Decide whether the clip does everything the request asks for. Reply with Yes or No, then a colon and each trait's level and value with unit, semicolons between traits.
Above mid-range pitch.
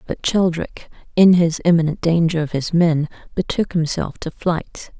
No: medium, 165 Hz